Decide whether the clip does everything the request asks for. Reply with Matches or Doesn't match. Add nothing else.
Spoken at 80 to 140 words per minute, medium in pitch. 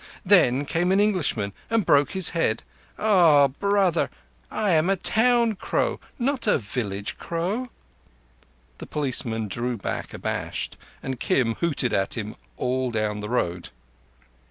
Matches